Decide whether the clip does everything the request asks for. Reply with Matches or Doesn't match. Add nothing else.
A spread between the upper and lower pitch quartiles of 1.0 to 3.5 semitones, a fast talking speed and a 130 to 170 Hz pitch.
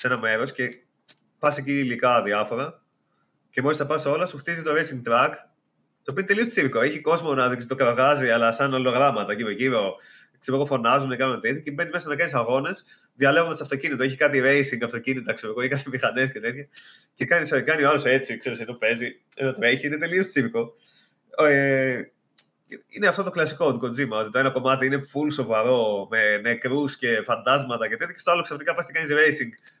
Matches